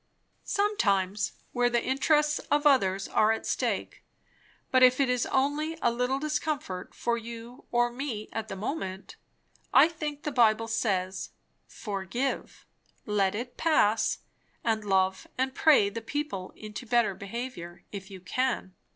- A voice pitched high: Yes, high, 235 Hz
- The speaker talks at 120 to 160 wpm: Yes, average, 140 wpm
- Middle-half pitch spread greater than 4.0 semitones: Yes, average, 5.1 semitones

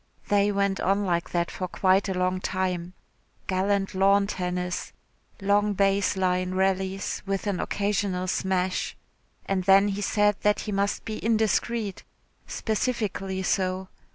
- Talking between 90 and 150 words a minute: Yes, slow, 135 wpm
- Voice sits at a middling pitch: No, high, 195 Hz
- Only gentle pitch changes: Yes, narrow, 1.6 semitones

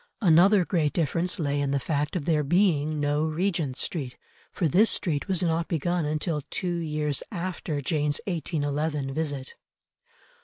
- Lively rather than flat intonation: No, average, 3.1 semitones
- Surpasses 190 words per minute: No, average, 150 wpm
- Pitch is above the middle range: No, medium, 155 Hz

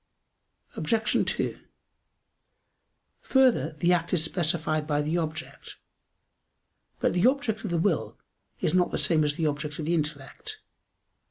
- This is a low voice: No, medium, 165 Hz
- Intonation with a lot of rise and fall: No, average, 3.3 semitones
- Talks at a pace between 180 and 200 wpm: No, average, 140 wpm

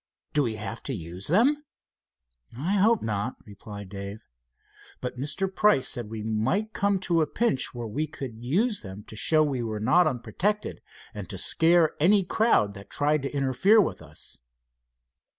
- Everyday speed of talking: Yes, average, 170 wpm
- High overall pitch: No, low, 135 Hz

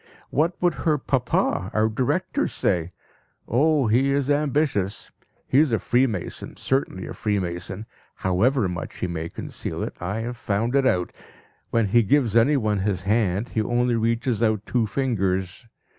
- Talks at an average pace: Yes, average, 155 wpm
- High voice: No, low, 115 Hz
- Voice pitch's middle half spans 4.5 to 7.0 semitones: Yes, average, 5.3 semitones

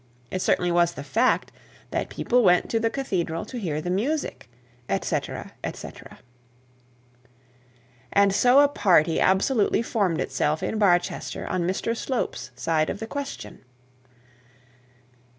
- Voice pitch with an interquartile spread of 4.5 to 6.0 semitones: Yes, average, 5.3 semitones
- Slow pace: Yes, slow, 130 wpm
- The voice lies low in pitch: No, high, 190 Hz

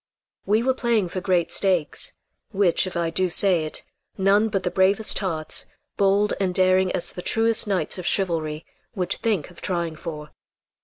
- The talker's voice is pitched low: No, medium, 185 Hz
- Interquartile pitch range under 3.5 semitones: Yes, average, 2.7 semitones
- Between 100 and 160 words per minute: No, average, 170 wpm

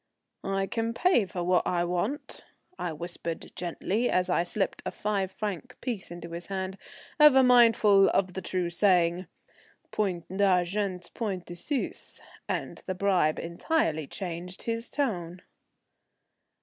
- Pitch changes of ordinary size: Yes, average, 3.3 semitones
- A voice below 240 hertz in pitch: Yes, medium, 185 Hz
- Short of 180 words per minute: Yes, slow, 135 wpm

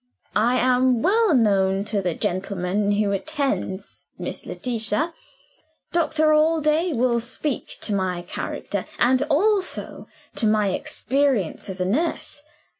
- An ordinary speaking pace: No, slow, 120 wpm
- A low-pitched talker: No, high, 235 Hz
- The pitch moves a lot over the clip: Yes, wide, 7.6 semitones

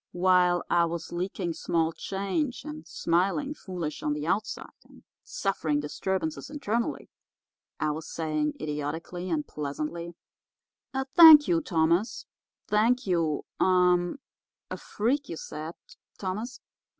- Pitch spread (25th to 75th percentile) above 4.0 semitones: Yes, average, 5.1 semitones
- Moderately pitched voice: Yes, medium, 175 Hz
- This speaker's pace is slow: Yes, slow, 105 wpm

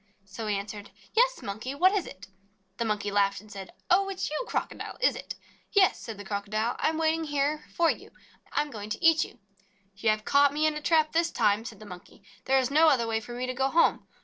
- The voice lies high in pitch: Yes, very high, 255 Hz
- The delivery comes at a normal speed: No, fast, 245 wpm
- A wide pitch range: Yes, wide, 7.0 semitones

